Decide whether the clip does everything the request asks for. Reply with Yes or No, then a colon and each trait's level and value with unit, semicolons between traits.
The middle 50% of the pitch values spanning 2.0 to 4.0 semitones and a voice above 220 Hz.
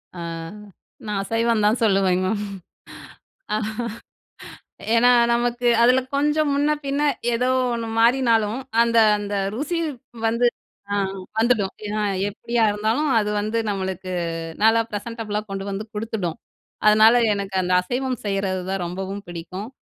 No: average, 3.2 semitones; high, 215 Hz